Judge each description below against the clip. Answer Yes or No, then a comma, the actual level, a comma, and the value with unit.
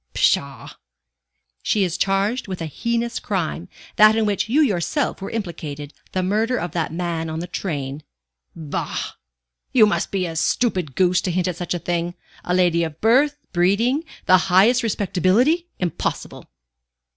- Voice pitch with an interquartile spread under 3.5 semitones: No, average, 4.3 semitones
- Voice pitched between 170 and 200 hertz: Yes, medium, 185 Hz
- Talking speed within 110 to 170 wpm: Yes, average, 155 wpm